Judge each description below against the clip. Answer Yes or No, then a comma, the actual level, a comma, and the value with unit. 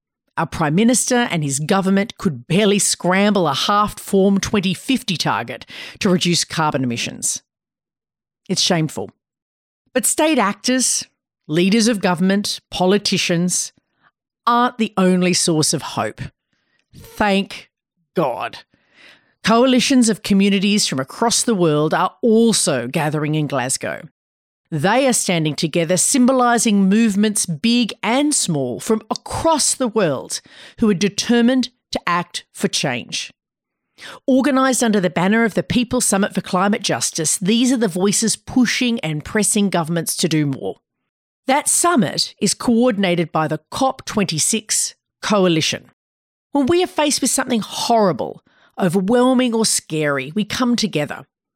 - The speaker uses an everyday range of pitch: No, wide, 5.7 semitones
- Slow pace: Yes, slow, 130 wpm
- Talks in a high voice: Yes, high, 200 Hz